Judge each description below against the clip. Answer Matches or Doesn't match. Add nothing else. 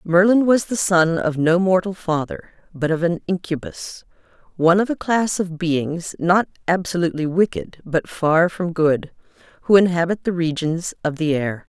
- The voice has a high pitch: Doesn't match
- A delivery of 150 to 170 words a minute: Matches